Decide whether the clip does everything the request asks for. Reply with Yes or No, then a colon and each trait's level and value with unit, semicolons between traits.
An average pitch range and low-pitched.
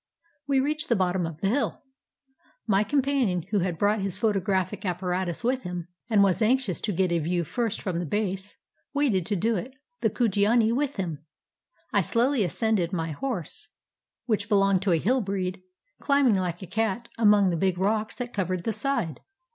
No: average, 4.3 semitones; high, 200 Hz